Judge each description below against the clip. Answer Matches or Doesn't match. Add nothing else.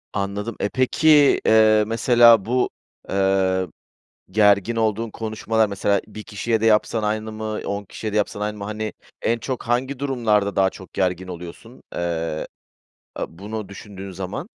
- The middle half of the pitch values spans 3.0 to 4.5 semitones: Doesn't match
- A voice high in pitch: Doesn't match